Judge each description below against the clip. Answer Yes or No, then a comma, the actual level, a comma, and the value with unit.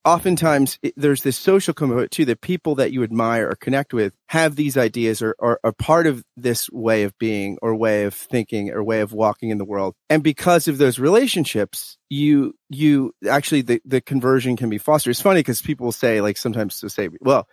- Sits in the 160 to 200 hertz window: No, low, 125 Hz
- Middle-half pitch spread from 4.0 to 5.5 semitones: Yes, average, 5.1 semitones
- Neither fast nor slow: No, fast, 210 wpm